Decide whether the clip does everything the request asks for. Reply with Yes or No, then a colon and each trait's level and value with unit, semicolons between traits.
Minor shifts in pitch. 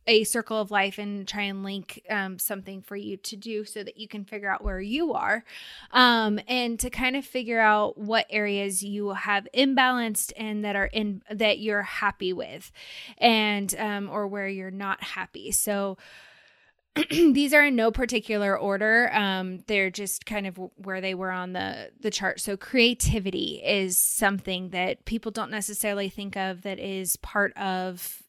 Yes: narrow, 2.2 semitones